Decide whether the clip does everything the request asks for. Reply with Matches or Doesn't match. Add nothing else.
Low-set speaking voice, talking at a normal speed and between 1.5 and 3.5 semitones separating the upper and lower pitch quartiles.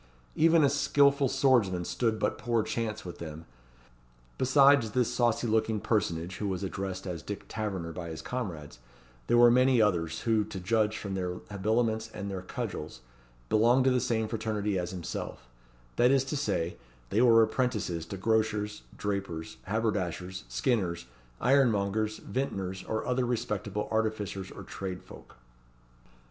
Doesn't match